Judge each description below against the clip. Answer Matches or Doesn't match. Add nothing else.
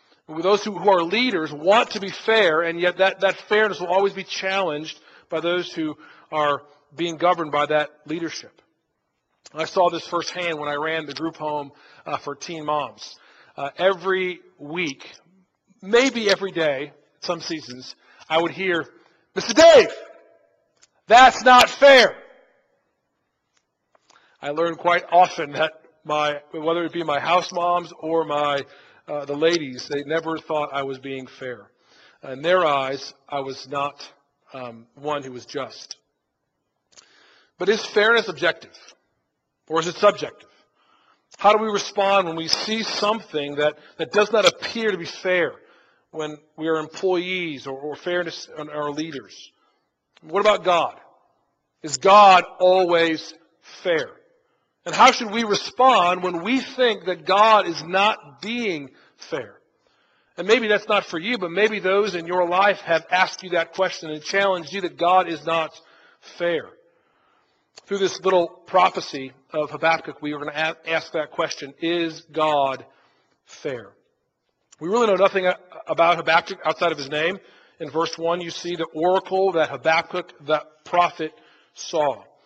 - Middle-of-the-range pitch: Matches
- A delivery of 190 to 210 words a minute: Doesn't match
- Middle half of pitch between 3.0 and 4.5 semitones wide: Matches